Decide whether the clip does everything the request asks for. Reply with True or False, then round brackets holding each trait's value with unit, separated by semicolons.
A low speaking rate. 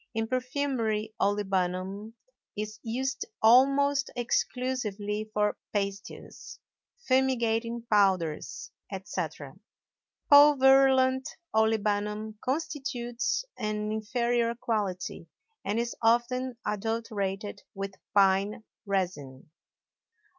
True (75 wpm)